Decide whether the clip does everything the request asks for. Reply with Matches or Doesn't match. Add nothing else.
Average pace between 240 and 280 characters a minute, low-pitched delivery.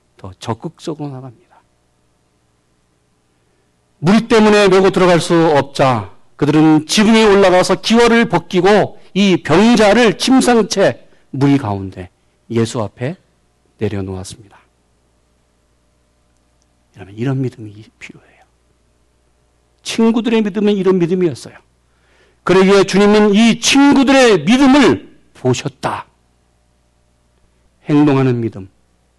Doesn't match